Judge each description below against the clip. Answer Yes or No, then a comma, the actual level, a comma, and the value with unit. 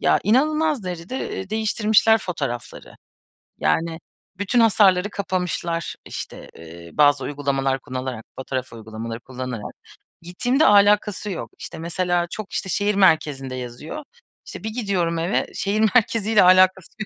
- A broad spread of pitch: Yes, wide, 7.5 semitones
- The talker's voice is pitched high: No, medium, 180 Hz